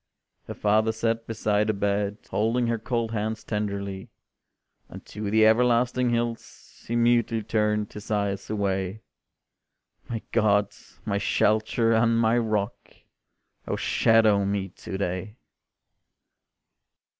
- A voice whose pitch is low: Yes, low, 110 Hz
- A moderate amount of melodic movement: No, narrow, 2.0 semitones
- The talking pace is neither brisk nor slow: No, slow, 120 wpm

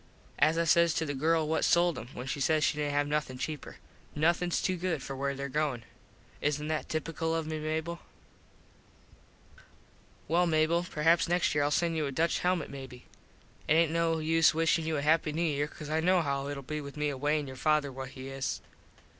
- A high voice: No, medium, 155 Hz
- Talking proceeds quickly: Yes, fast, 210 wpm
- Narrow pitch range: Yes, narrow, 2.3 semitones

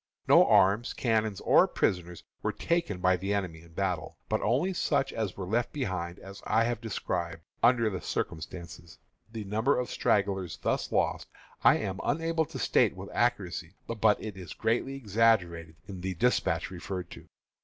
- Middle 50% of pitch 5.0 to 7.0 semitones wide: No, average, 4.3 semitones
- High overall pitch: No, low, 100 Hz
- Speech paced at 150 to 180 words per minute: Yes, average, 165 wpm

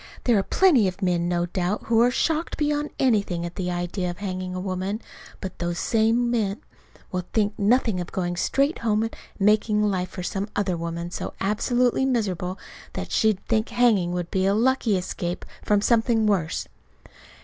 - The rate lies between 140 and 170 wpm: No, average, 180 wpm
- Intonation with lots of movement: No, average, 4.0 semitones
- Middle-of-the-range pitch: No, high, 200 Hz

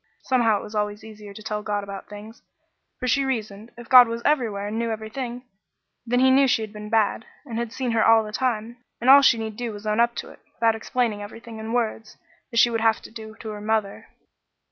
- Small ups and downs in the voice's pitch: Yes, narrow, 2.0 semitones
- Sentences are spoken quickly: Yes, fast, 240 wpm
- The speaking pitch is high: Yes, high, 225 Hz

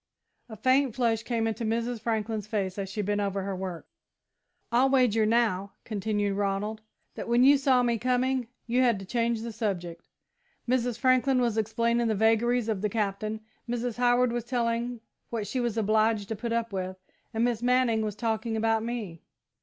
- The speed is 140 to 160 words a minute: No, average, 180 wpm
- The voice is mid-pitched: No, high, 225 Hz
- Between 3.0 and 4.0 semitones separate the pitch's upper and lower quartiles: No, narrow, 2.4 semitones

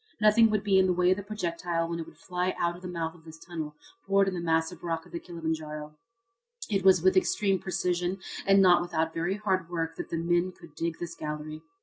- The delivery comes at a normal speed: No, fast, 230 wpm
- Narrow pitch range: Yes, narrow, 2.3 semitones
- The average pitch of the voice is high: No, medium, 175 Hz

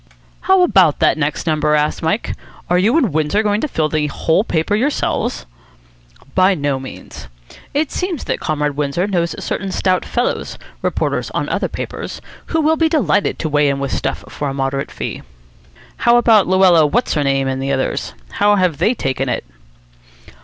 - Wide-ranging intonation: Yes, wide, 6.6 semitones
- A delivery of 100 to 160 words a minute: No, average, 180 wpm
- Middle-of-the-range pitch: Yes, medium, 170 Hz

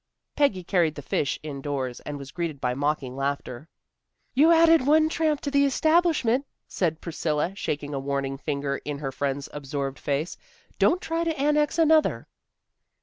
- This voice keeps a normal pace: Yes, average, 155 wpm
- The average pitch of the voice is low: No, medium, 155 Hz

